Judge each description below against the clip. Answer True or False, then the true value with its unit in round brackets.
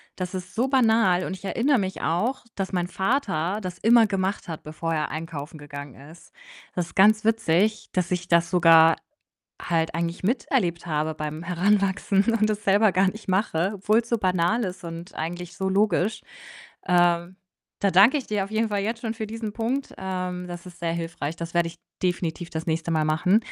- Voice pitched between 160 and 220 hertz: True (185 Hz)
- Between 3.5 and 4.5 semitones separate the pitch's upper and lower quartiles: True (4.0 semitones)